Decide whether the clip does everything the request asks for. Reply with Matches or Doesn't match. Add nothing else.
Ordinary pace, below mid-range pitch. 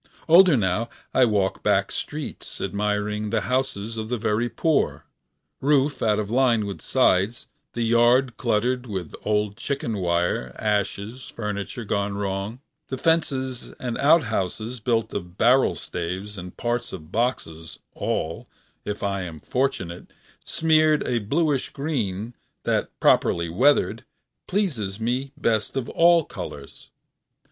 Doesn't match